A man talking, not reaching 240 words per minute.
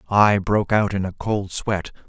Yes: male; average, 200 wpm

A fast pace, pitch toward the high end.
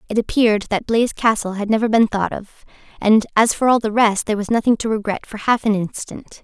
Yes: fast, 235 wpm; high, 215 Hz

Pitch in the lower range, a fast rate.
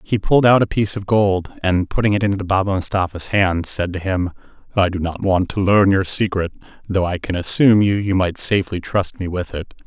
Yes: very low, 95 Hz; fast, 225 wpm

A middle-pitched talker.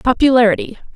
No: high, 240 Hz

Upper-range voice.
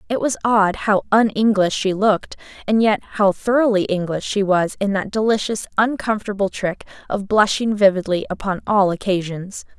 Yes: high, 205 Hz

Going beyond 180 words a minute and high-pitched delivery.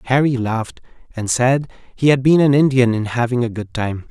No: fast, 205 wpm; low, 125 Hz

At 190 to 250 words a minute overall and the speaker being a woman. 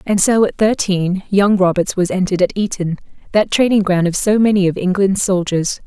Yes: average, 195 wpm; female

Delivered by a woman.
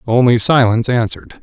No: male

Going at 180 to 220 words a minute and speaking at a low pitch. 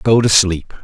Yes: fast, 215 wpm; low, 100 Hz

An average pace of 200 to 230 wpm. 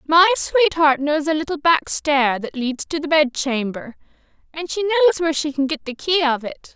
Yes: fast, 205 wpm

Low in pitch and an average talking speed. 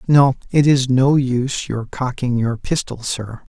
Yes: low, 130 Hz; average, 170 wpm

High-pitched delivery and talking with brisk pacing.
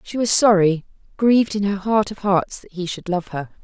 Yes: high, 195 Hz; fast, 230 wpm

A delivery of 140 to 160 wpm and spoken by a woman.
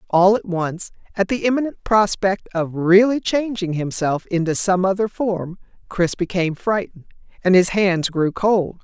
Yes: average, 155 wpm; female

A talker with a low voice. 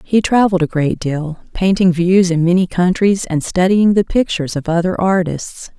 No: medium, 180 Hz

